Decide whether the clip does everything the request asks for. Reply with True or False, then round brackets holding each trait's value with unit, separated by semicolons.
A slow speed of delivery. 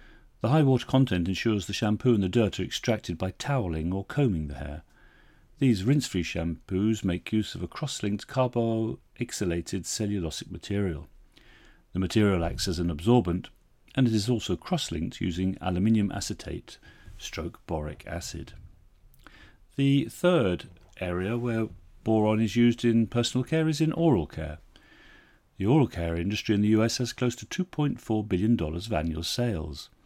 False (155 wpm)